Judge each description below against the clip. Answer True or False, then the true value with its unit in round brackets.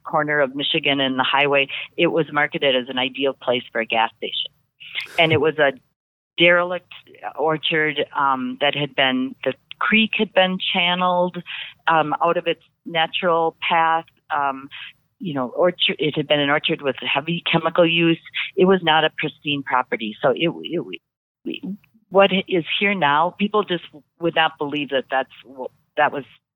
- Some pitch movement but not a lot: True (3.8 semitones)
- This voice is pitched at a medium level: True (155 Hz)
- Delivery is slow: False (165 wpm)